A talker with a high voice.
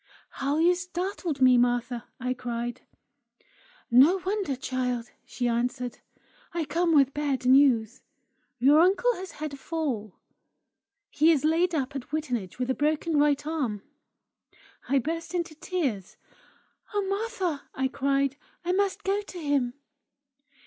Yes: very high, 285 Hz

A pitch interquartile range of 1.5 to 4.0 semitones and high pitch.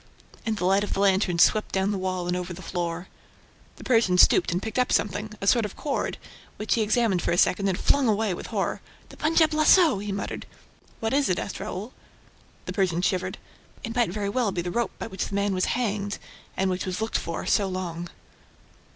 Yes: average, 3.3 semitones; high, 200 Hz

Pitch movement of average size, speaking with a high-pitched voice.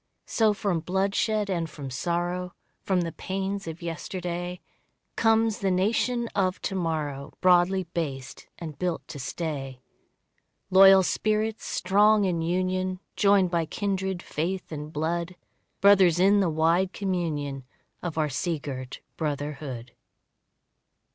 No: average, 3.4 semitones; medium, 180 Hz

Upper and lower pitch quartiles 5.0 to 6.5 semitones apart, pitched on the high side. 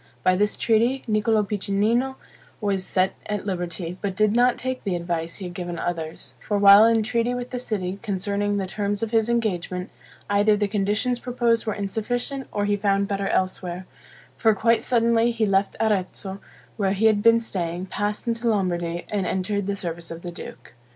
No: average, 3.3 semitones; high, 205 Hz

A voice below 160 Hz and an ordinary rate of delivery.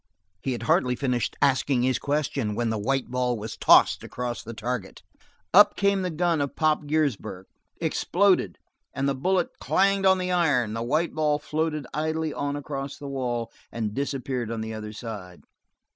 Yes: low, 135 Hz; average, 175 wpm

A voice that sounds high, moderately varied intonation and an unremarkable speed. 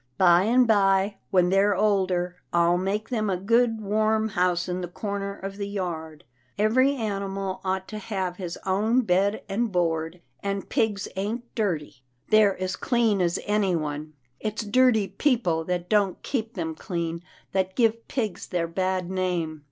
Yes: high, 195 Hz; average, 3.2 semitones; average, 160 wpm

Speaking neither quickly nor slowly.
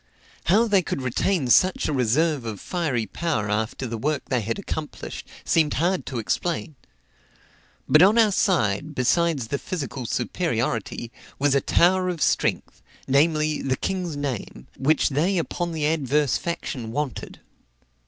Yes: average, 145 wpm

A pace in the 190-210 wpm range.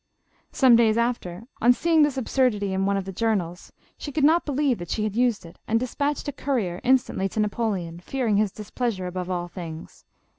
Yes: average, 200 wpm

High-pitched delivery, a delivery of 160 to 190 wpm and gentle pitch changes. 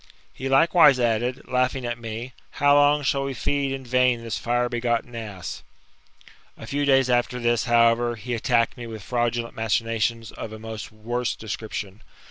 No: low, 120 Hz; average, 170 wpm; narrow, 2.1 semitones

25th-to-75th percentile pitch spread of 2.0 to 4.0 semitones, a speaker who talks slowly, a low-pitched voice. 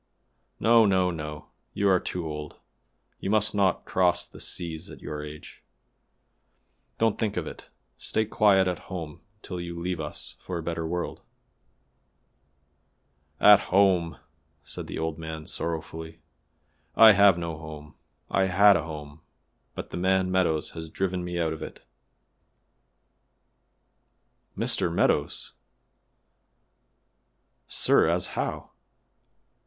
Yes: average, 3.0 semitones; slow, 125 wpm; very low, 85 Hz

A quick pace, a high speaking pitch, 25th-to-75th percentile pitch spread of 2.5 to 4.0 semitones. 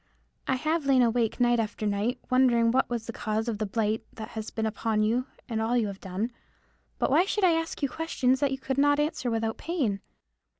Yes: fast, 220 wpm; high, 240 Hz; average, 3.4 semitones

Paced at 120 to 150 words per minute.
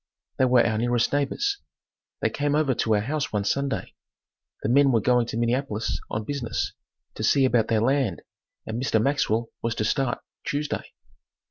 No: average, 170 wpm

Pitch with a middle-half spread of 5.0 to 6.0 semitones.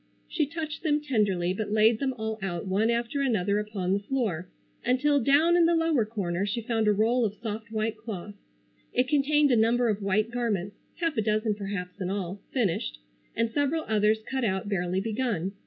No: average, 4.2 semitones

